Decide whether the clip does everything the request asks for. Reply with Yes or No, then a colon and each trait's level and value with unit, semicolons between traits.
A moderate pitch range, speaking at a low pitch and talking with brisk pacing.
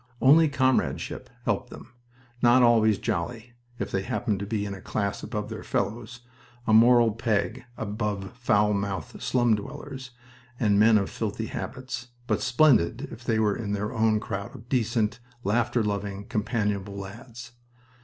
No: average, 3.0 semitones; low, 110 Hz; average, 150 wpm